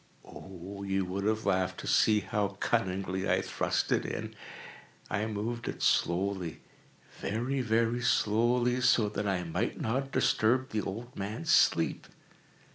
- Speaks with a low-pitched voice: Yes, low, 105 Hz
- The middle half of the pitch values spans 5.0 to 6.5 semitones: No, average, 3.3 semitones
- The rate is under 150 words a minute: Yes, slow, 135 wpm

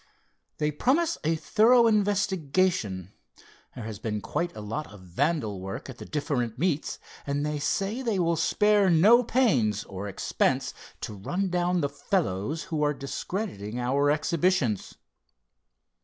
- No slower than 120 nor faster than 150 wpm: Yes, average, 140 wpm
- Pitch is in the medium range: Yes, medium, 150 Hz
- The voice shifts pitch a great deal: Yes, wide, 8.5 semitones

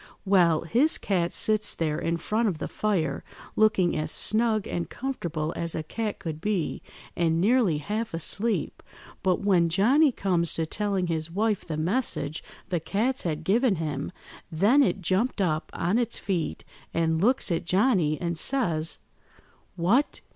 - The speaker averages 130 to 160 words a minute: Yes, average, 155 wpm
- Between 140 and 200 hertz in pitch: Yes, medium, 185 Hz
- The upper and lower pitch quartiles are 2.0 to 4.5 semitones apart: No, average, 4.9 semitones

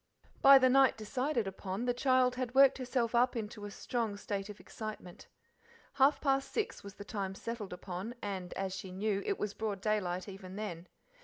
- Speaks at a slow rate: No, average, 185 wpm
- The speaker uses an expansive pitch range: No, average, 4.5 semitones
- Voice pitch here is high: Yes, high, 215 Hz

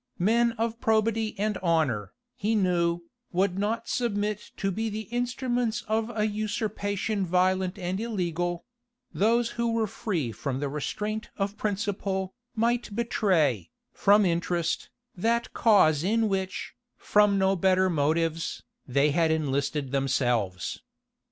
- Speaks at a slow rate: Yes, slow, 125 wpm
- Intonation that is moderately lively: Yes, average, 4.5 semitones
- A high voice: Yes, high, 195 Hz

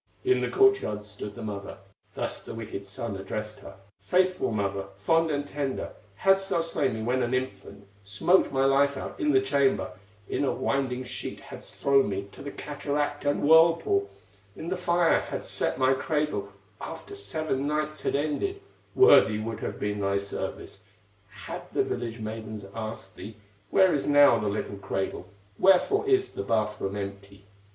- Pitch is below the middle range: Yes, low, 130 Hz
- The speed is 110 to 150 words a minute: No, average, 175 wpm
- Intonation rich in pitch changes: Yes, wide, 6.8 semitones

